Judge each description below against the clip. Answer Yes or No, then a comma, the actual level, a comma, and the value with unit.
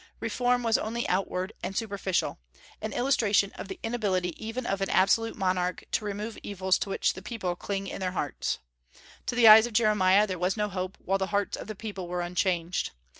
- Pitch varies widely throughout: No, average, 2.9 semitones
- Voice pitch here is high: Yes, high, 195 Hz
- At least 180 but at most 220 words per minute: Yes, average, 200 wpm